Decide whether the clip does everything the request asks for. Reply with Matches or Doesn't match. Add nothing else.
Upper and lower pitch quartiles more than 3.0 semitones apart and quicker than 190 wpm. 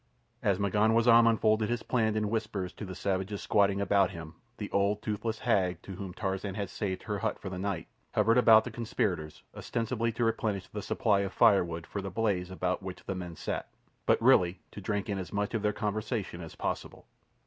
Doesn't match